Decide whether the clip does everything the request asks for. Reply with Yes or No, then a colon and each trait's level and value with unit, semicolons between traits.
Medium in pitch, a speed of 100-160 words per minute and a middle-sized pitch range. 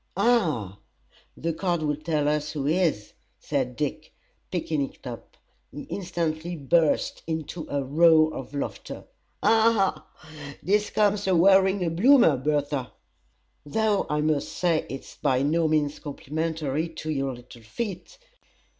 Yes: medium, 155 Hz; average, 140 wpm; average, 3.6 semitones